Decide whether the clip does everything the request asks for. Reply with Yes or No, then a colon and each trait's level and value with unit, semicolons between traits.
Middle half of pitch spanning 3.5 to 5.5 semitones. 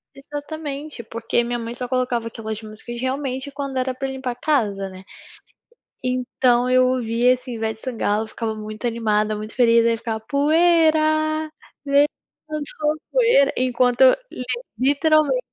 Yes: average, 3.9 semitones